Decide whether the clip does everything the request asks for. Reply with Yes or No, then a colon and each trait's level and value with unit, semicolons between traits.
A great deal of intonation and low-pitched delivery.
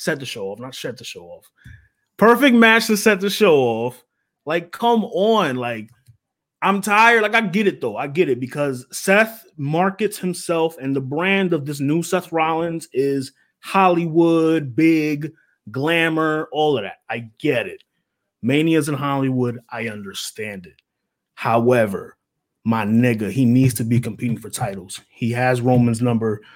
No: wide, 7.0 semitones; medium, 150 Hz